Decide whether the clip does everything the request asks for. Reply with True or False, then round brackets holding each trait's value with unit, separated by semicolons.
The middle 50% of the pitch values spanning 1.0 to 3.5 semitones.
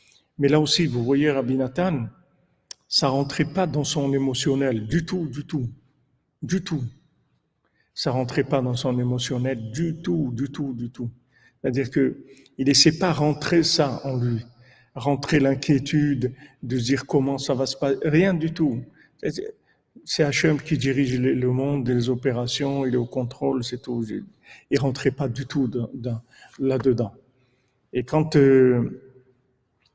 True (2.7 semitones)